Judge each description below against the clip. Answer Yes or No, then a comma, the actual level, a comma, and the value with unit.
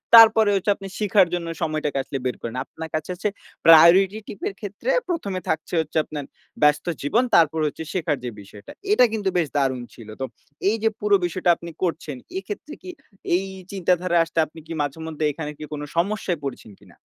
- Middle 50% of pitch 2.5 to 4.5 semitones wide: No, average, 5.0 semitones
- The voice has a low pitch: No, medium, 170 Hz